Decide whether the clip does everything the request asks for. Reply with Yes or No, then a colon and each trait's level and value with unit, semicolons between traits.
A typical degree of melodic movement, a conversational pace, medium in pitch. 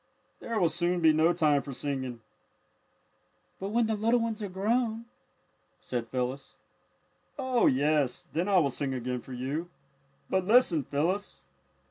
No: wide, 7.5 semitones; average, 150 wpm; medium, 170 Hz